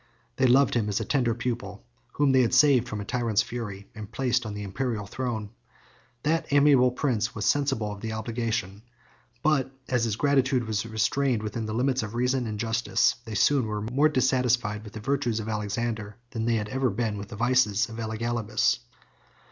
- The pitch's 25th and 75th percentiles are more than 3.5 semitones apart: No, average, 3.2 semitones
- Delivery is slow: No, average, 190 wpm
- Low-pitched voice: Yes, low, 115 Hz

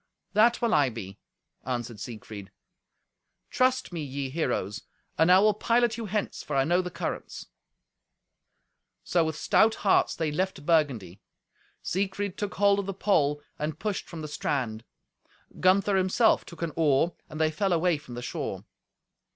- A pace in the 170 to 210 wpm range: No, average, 160 wpm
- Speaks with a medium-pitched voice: Yes, medium, 165 Hz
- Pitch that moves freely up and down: Yes, wide, 6.1 semitones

